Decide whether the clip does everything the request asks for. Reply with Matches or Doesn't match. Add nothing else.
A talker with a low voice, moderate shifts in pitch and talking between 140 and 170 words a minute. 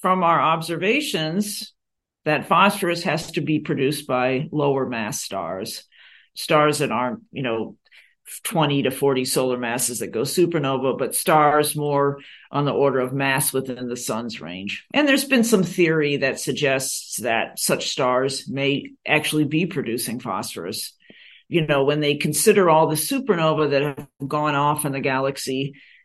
Doesn't match